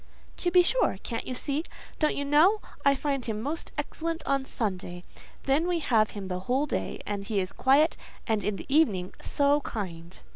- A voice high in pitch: Yes, very high, 270 Hz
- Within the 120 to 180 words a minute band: No, fast, 205 wpm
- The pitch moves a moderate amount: No, wide, 6.6 semitones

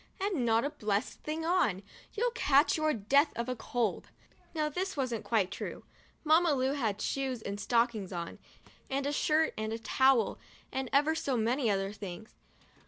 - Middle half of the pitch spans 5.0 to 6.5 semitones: Yes, wide, 5.6 semitones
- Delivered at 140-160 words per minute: No, average, 170 wpm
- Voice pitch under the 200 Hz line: No, very high, 255 Hz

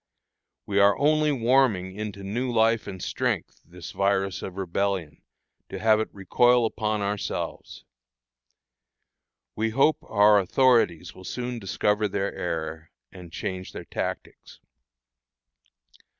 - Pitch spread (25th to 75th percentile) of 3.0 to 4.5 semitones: Yes, average, 3.4 semitones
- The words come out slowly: Yes, slow, 120 wpm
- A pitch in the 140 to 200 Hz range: No, low, 100 Hz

